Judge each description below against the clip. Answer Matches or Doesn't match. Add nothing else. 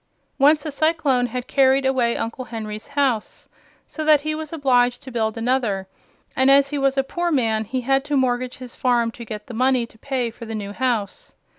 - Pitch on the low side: Doesn't match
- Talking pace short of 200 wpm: Doesn't match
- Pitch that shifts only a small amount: Doesn't match